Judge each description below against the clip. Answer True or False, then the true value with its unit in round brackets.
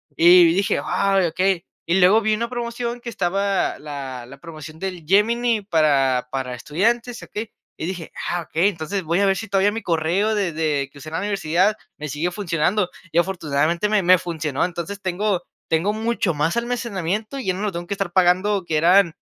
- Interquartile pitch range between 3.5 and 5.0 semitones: True (4.2 semitones)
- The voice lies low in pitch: False (180 Hz)